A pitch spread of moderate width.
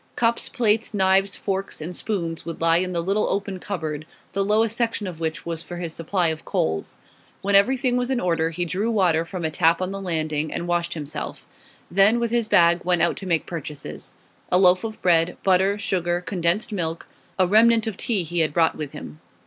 Yes: average, 3.4 semitones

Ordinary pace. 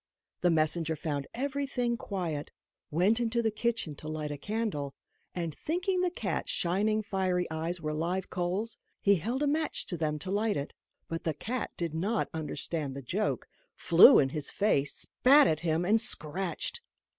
Yes: average, 170 wpm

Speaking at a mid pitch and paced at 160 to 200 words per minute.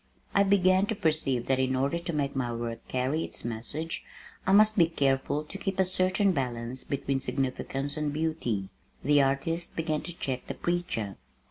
Yes: medium, 145 Hz; average, 175 wpm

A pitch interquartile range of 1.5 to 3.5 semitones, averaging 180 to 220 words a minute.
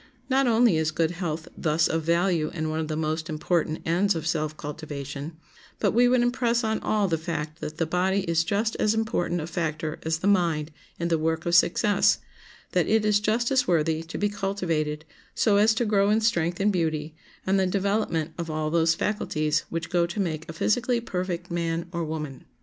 No: average, 4.3 semitones; fast, 205 wpm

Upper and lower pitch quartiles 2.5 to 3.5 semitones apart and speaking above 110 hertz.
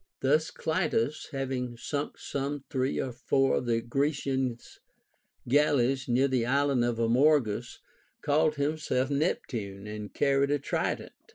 Yes: average, 3.1 semitones; low, 135 Hz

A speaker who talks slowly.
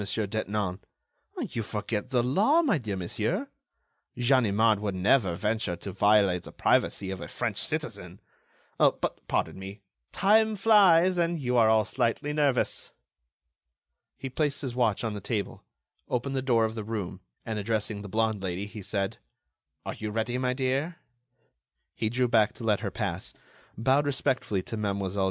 No: average, 160 wpm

